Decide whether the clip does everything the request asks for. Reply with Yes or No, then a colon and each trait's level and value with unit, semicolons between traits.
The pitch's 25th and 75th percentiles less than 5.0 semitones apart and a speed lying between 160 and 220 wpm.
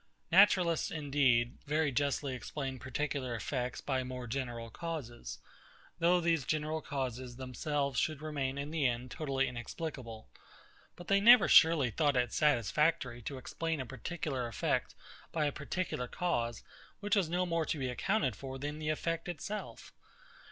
No: average, 4.2 semitones; average, 150 wpm